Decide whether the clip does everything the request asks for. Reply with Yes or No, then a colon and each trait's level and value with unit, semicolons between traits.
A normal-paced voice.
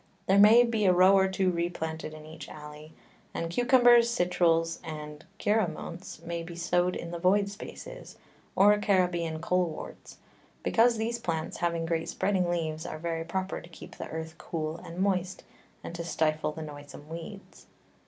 Yes: average, 165 wpm